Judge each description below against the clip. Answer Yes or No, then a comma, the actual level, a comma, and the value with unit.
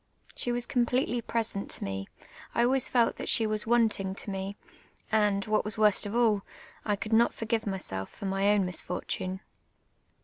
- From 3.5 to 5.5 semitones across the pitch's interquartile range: No, average, 3.0 semitones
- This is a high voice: Yes, high, 210 Hz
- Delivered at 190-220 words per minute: No, average, 175 wpm